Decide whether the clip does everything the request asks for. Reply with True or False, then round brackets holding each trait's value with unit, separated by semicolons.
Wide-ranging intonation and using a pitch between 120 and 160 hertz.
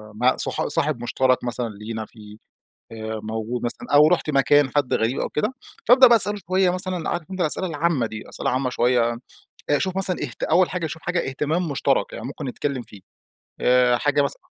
True (6.5 semitones; 140 Hz)